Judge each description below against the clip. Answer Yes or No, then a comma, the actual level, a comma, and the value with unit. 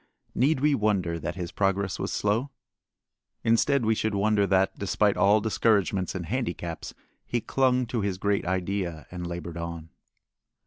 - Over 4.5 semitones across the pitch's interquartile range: No, average, 3.9 semitones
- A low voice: Yes, low, 100 Hz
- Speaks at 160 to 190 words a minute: No, average, 150 wpm